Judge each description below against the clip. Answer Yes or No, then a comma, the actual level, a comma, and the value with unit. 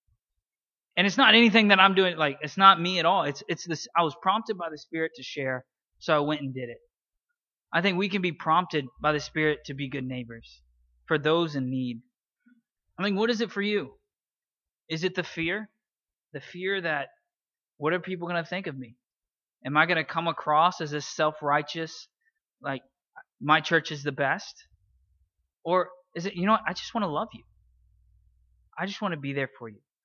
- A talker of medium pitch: Yes, medium, 160 Hz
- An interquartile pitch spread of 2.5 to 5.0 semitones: No, wide, 5.5 semitones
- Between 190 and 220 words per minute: Yes, average, 200 wpm